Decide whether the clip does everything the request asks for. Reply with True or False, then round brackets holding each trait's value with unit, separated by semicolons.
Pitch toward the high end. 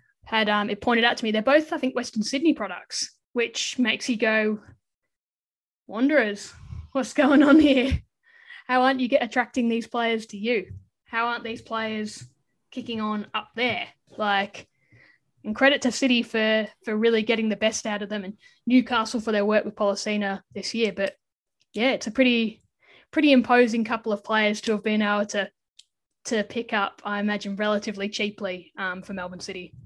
True (220 Hz)